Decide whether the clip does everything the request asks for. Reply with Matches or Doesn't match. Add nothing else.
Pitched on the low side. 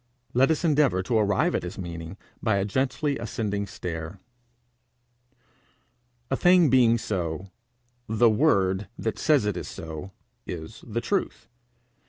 Matches